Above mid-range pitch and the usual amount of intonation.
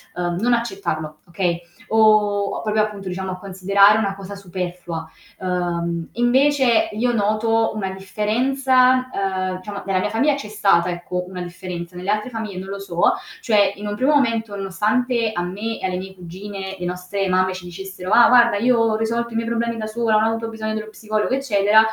Yes: high, 205 Hz; average, 3.5 semitones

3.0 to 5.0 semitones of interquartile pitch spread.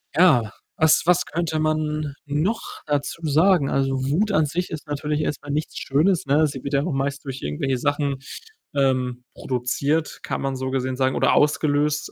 No: narrow, 2.5 semitones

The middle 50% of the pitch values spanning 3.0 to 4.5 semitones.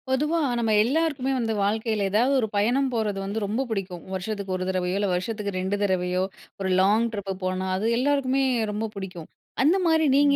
No: average, 5.2 semitones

